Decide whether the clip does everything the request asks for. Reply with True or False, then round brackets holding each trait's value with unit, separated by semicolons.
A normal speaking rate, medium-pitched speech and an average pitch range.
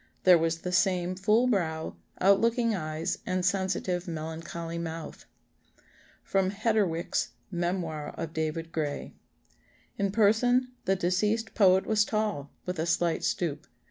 False (130 wpm; 180 Hz; 3.6 semitones)